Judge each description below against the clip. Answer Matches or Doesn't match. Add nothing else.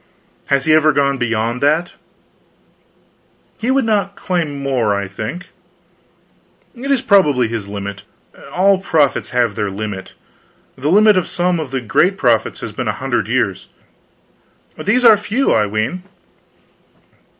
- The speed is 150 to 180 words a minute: Doesn't match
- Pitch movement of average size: Doesn't match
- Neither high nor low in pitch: Matches